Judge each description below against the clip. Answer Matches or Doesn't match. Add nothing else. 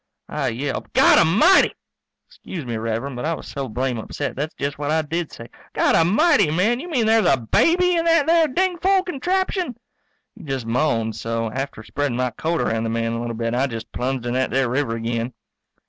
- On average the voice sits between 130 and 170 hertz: Matches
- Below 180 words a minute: Doesn't match